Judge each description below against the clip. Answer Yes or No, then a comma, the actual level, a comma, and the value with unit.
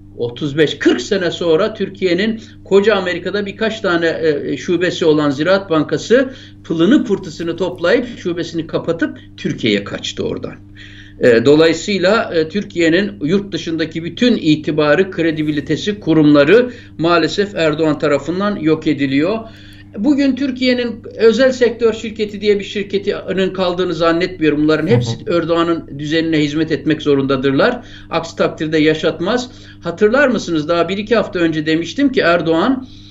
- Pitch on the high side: No, medium, 170 Hz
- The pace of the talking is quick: No, average, 115 wpm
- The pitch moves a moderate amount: Yes, average, 4.8 semitones